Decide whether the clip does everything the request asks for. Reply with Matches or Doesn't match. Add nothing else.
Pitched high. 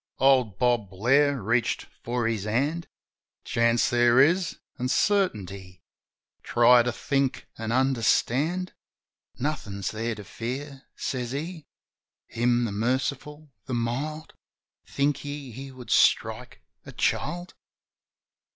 Doesn't match